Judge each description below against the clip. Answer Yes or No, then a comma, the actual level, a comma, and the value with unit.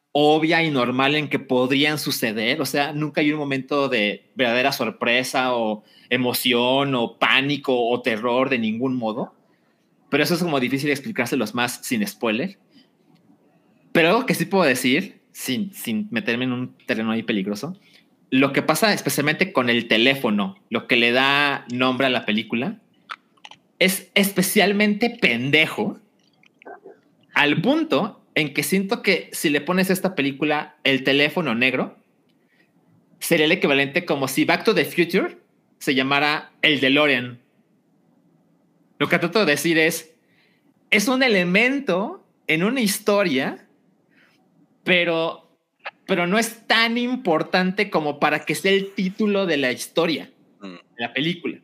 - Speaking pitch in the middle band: Yes, medium, 150 Hz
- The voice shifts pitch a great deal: Yes, wide, 6.4 semitones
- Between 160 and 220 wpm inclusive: No, average, 145 wpm